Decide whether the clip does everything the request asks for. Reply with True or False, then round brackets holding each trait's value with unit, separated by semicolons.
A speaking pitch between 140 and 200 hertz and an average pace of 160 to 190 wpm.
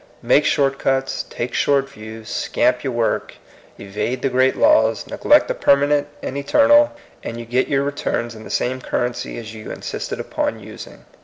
False (130 Hz; 170 wpm)